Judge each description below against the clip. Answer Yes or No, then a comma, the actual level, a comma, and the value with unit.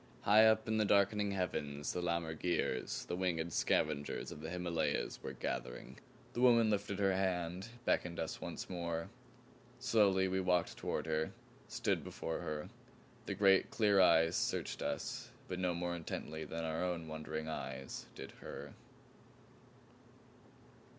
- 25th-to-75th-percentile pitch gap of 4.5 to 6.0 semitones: No, average, 3.4 semitones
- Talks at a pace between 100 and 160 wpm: Yes, average, 145 wpm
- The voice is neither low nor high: No, very low, 90 Hz